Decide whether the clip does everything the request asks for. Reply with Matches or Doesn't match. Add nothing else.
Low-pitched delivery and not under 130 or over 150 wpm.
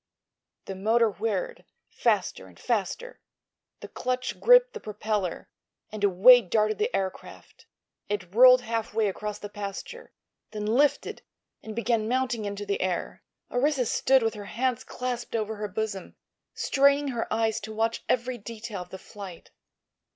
Doesn't match